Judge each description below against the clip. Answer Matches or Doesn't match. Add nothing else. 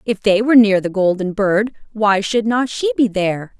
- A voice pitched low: Doesn't match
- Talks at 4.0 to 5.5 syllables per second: Matches